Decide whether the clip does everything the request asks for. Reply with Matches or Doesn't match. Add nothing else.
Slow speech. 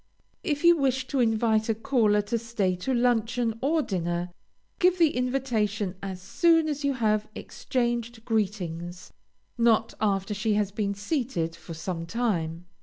Doesn't match